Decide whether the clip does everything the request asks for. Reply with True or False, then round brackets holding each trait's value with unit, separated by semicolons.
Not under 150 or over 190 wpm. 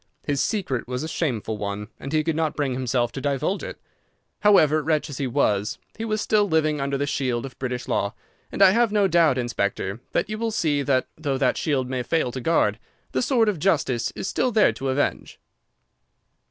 False (205 wpm)